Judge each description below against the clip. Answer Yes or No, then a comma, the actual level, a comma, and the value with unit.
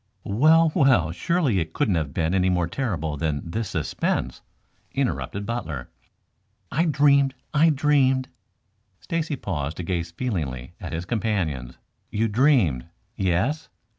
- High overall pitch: No, low, 100 Hz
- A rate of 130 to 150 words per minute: Yes, slow, 135 wpm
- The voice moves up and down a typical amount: No, wide, 8.7 semitones